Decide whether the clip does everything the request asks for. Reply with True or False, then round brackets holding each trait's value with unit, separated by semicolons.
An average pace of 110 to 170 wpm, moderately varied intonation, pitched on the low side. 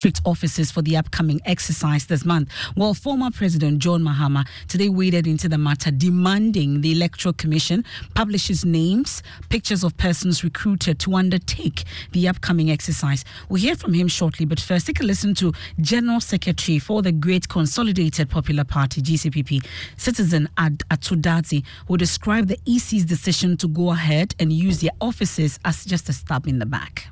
False (165 wpm; 3.2 semitones; 170 Hz)